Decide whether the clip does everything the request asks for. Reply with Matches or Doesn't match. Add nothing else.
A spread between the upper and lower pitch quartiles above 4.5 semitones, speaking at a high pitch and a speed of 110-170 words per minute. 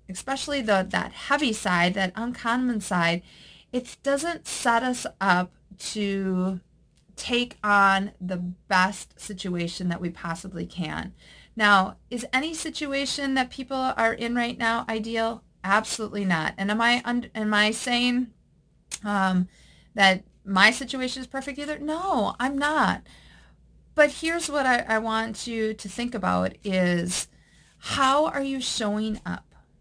Matches